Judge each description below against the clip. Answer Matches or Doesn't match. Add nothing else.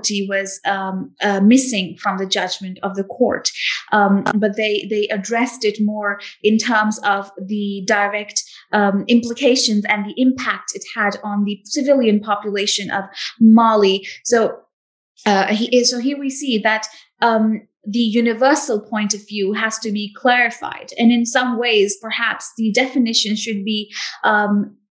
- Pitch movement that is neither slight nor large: Doesn't match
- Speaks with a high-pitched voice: Matches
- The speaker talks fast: Doesn't match